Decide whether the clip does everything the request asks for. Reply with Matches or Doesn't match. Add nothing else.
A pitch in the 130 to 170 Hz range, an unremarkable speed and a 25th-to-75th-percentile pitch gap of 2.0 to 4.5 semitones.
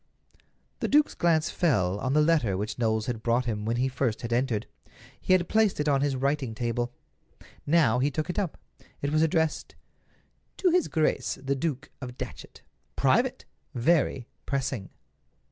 Doesn't match